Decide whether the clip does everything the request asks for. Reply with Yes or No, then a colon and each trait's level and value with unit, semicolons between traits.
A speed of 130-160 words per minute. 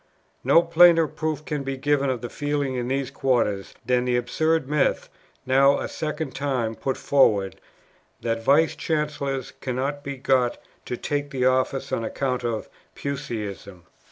Yes: average, 155 wpm